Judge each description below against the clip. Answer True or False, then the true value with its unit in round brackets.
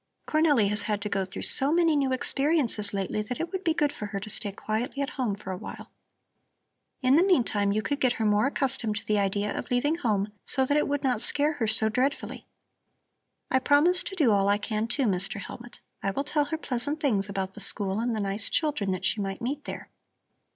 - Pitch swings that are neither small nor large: False (5.9 semitones)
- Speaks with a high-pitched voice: True (235 Hz)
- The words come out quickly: True (230 wpm)